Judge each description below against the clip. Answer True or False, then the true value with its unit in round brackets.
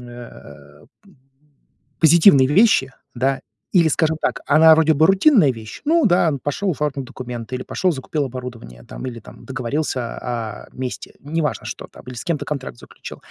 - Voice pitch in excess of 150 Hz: False (135 Hz)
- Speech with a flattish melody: False (4.7 semitones)